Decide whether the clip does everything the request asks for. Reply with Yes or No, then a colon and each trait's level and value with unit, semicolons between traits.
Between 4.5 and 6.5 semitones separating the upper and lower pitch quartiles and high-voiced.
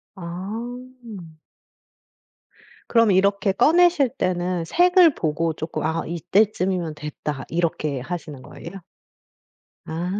No: wide, 5.5 semitones; medium, 180 Hz